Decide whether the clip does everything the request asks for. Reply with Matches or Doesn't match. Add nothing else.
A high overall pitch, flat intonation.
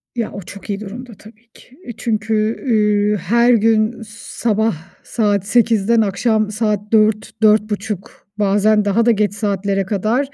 Matches